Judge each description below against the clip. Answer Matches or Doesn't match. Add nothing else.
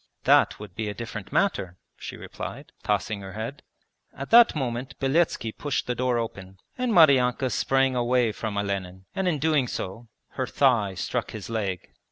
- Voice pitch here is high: Doesn't match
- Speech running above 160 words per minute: Matches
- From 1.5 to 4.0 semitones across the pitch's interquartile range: Doesn't match